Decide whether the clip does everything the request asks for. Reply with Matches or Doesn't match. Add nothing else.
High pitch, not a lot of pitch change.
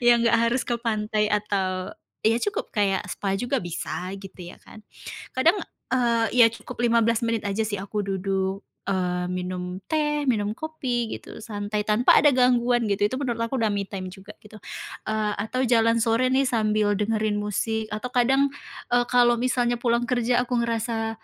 Doesn't match